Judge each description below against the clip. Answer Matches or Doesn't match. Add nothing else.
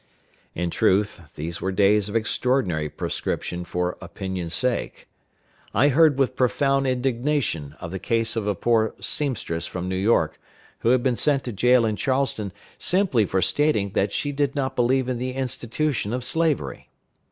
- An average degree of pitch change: Doesn't match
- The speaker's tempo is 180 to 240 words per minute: Doesn't match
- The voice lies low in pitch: Matches